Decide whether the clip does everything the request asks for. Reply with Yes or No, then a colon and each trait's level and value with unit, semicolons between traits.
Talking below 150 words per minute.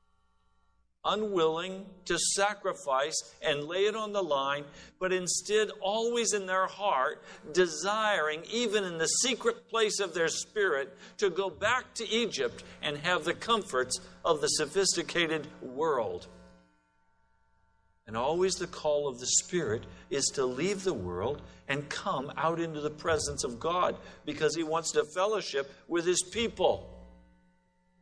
Yes: average, 140 wpm